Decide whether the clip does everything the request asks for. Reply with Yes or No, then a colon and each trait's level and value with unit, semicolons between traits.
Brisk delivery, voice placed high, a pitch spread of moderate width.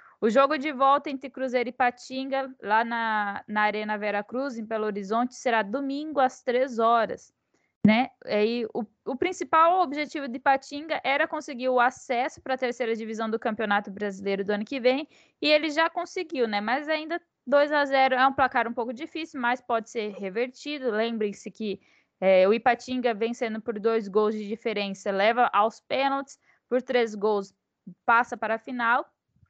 No: average, 175 wpm; high, 245 Hz; average, 3.9 semitones